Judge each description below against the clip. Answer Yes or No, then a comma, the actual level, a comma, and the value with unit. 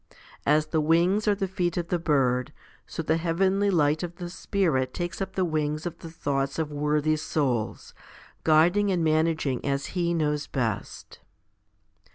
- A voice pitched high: No, medium, 160 Hz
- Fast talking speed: No, average, 165 wpm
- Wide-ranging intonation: No, average, 2.9 semitones